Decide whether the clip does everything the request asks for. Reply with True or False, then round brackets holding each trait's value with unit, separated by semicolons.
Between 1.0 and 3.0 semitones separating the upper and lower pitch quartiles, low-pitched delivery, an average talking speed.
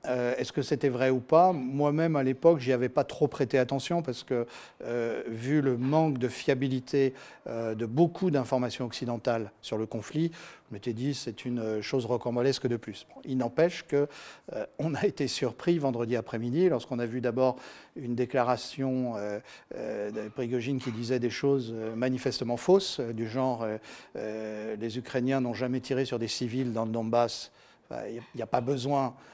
True (2.7 semitones; 125 Hz; 185 wpm)